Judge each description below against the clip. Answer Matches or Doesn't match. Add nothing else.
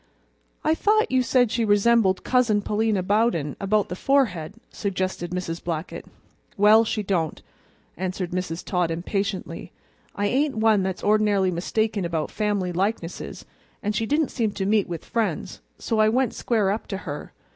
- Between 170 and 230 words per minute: Doesn't match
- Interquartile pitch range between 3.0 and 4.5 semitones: Matches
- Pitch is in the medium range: Doesn't match